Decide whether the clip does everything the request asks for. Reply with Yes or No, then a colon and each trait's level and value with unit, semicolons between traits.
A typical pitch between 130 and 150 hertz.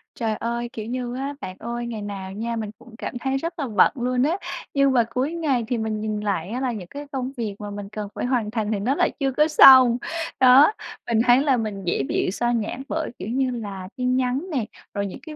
No: high, 240 Hz